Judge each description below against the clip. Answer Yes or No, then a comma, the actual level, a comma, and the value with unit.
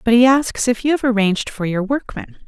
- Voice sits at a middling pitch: No, high, 230 Hz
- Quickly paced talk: Yes, fast, 240 wpm